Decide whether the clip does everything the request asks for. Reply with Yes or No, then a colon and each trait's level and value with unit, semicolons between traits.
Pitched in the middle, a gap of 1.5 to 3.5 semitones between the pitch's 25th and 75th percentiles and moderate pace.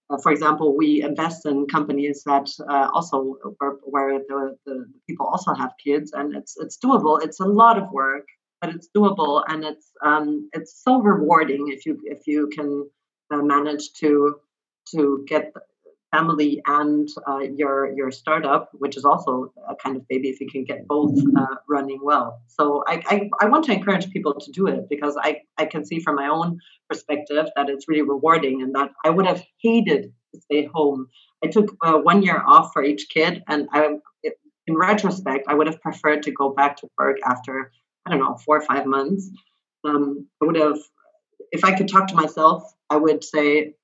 Yes: medium, 150 Hz; narrow, 2.6 semitones; average, 195 wpm